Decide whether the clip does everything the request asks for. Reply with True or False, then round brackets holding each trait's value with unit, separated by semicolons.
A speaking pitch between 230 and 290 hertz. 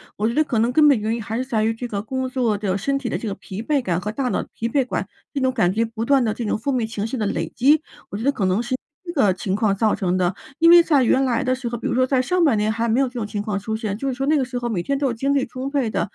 True (235 Hz)